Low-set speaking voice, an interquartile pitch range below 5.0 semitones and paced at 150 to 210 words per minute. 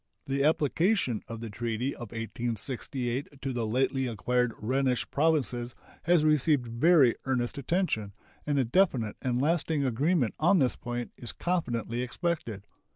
No: low, 130 Hz; average, 4.3 semitones; average, 140 wpm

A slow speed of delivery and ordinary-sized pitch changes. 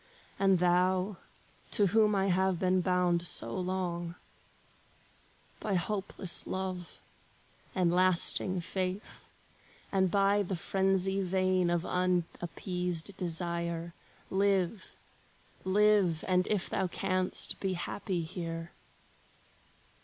No: slow, 100 wpm; narrow, 1.7 semitones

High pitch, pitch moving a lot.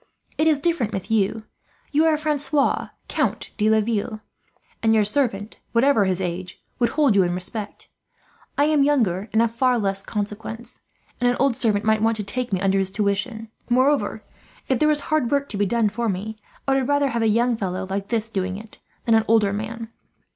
No: high, 225 Hz; average, 4.1 semitones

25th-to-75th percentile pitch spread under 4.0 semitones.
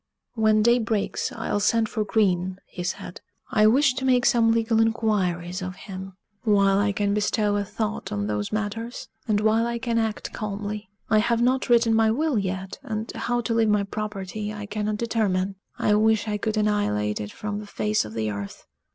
Yes: narrow, 2.6 semitones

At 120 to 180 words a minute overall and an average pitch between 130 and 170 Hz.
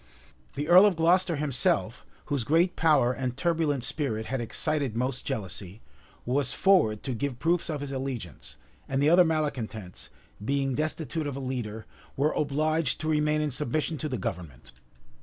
Yes: average, 160 wpm; medium, 140 Hz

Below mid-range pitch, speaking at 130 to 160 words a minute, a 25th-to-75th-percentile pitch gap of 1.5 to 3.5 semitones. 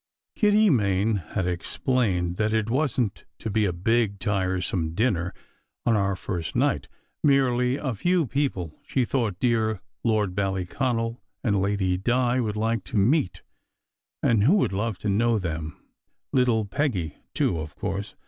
No: low, 110 Hz; average, 150 wpm; average, 4.6 semitones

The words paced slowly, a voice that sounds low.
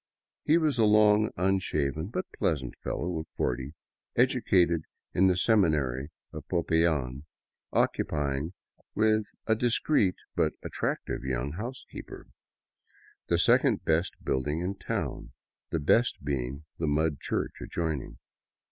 Yes: slow, 125 wpm; very low, 85 Hz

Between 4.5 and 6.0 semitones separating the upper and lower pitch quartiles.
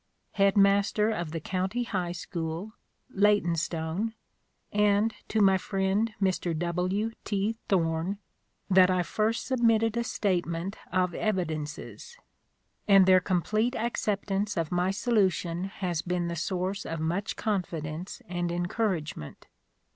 No: average, 3.3 semitones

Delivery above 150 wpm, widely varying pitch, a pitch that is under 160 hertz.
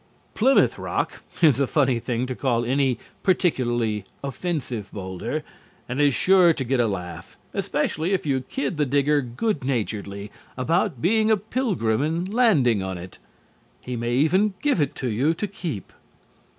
Yes: average, 160 wpm; wide, 6.9 semitones; low, 135 Hz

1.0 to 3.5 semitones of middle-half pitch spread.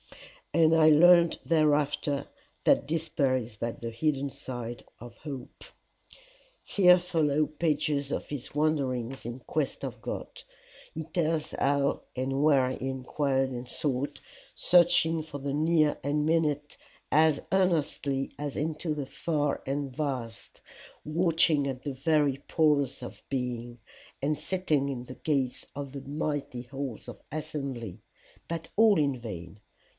Yes: average, 2.9 semitones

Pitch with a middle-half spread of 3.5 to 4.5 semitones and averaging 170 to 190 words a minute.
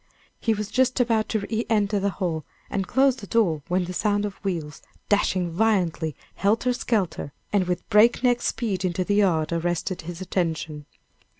Yes: average, 4.0 semitones; average, 175 wpm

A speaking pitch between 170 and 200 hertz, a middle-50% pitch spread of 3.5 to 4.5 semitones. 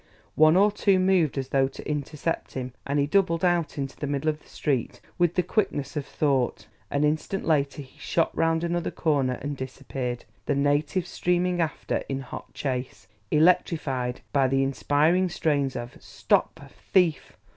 No: medium, 150 Hz; average, 3.9 semitones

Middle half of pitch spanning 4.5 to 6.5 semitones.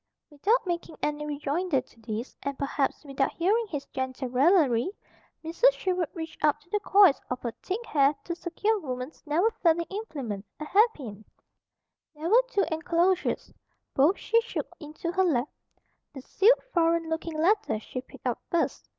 Yes: wide, 5.4 semitones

